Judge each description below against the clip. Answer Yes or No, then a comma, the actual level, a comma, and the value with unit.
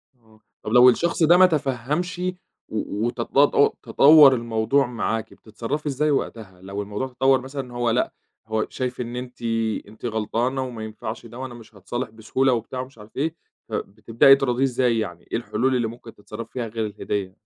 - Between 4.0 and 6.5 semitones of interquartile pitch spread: No, average, 3.2 semitones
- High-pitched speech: No, low, 120 Hz